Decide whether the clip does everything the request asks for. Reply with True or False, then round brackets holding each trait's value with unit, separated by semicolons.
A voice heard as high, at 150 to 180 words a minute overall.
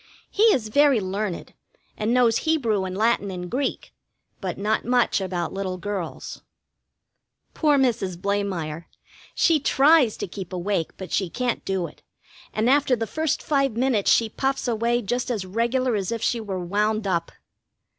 True (215 Hz; 160 wpm)